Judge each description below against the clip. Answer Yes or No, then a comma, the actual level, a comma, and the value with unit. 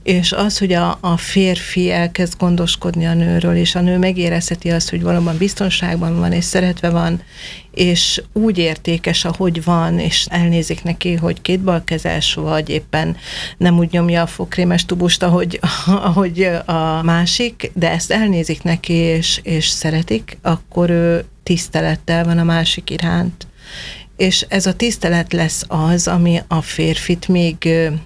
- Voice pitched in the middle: Yes, medium, 170 Hz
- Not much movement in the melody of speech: Yes, narrow, 1.2 semitones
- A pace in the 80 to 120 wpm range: No, average, 150 wpm